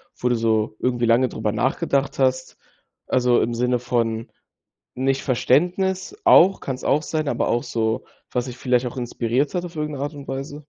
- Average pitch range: Yes, average, 3.2 semitones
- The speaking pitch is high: No, low, 130 Hz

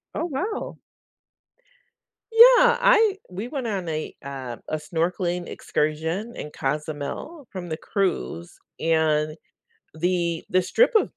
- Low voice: No, medium, 175 Hz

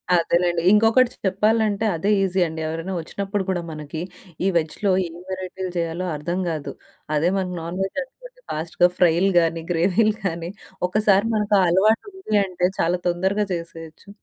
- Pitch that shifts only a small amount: No, average, 3.7 semitones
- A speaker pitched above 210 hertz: No, medium, 185 Hz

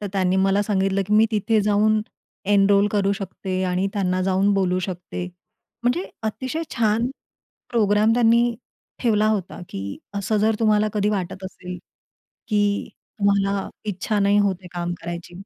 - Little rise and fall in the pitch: Yes, narrow, 2.1 semitones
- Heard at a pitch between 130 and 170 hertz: No, high, 200 Hz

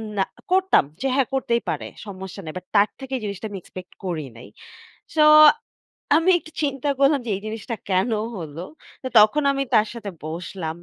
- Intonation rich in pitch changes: Yes, wide, 6.7 semitones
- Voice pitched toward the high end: Yes, high, 210 Hz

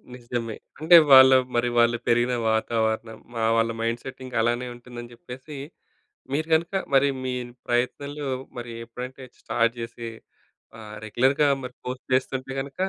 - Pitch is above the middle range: No, low, 120 Hz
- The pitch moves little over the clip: Yes, narrow, 2.2 semitones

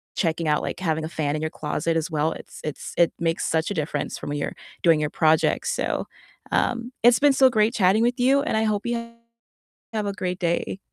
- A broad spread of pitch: Yes, wide, 6.3 semitones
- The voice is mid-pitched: Yes, medium, 170 Hz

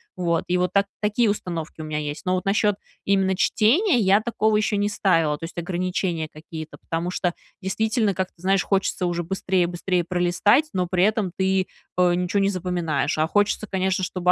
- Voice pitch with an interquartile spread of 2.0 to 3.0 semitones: Yes, narrow, 2.5 semitones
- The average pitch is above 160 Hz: Yes, medium, 185 Hz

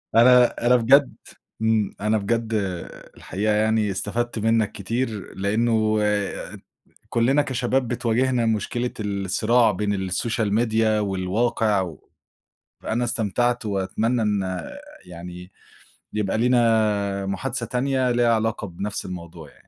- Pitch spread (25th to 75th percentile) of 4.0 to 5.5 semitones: No, average, 3.2 semitones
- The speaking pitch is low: Yes, low, 110 Hz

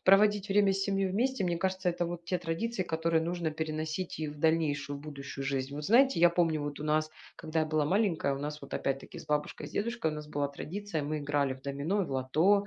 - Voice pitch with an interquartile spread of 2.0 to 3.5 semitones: No, average, 4.4 semitones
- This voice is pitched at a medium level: Yes, medium, 160 Hz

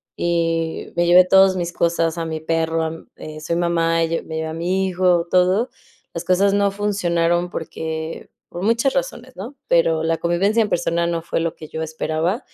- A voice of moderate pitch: Yes, medium, 170 Hz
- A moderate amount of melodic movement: No, narrow, 2.3 semitones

